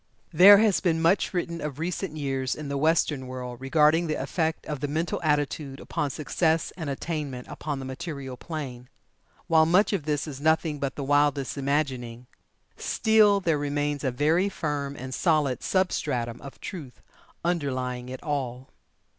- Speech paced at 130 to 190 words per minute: Yes, average, 160 wpm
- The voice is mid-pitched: Yes, medium, 145 Hz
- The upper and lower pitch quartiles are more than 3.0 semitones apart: Yes, average, 3.4 semitones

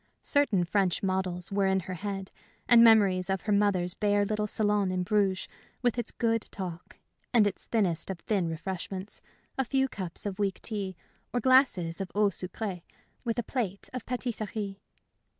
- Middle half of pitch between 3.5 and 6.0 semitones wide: No, average, 2.7 semitones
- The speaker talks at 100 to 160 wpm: No, average, 170 wpm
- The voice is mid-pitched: No, high, 200 Hz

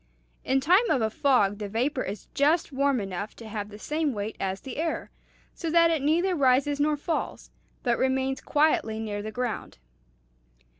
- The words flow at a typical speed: Yes, average, 180 wpm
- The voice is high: Yes, very high, 265 Hz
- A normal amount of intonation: No, wide, 5.7 semitones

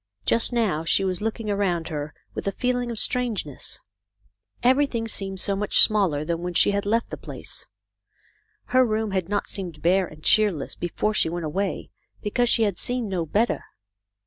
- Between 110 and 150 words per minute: No, average, 180 wpm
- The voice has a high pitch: Yes, high, 200 Hz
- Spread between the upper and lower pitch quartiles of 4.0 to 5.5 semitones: Yes, average, 4.5 semitones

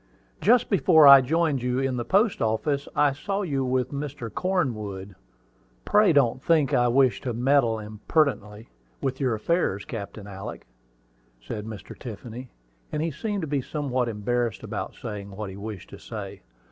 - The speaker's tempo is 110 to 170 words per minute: Yes, average, 160 wpm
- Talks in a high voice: No, low, 130 Hz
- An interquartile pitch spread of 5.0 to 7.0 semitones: Yes, average, 5.3 semitones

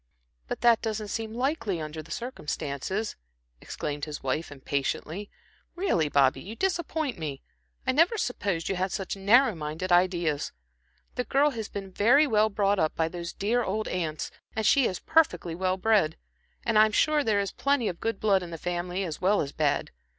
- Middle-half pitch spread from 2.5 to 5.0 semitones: No, wide, 5.6 semitones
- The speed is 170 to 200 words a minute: Yes, average, 180 wpm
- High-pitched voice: Yes, high, 195 Hz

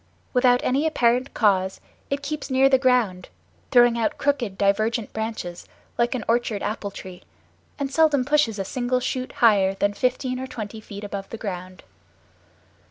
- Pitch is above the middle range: Yes, high, 235 Hz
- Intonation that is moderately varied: Yes, average, 4.1 semitones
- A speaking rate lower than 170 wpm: Yes, average, 160 wpm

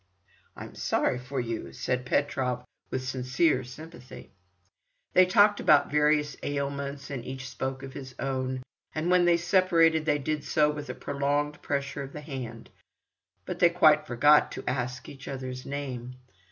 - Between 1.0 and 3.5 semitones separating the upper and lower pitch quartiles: Yes, average, 2.8 semitones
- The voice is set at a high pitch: No, medium, 140 Hz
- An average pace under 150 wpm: No, average, 155 wpm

